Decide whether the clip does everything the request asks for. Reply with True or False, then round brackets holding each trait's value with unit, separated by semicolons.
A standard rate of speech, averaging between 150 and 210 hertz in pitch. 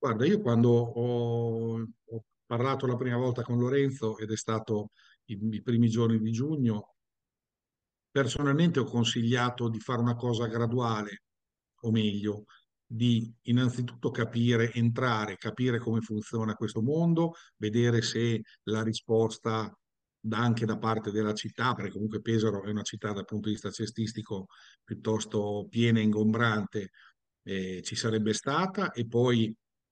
False (140 wpm; 115 Hz)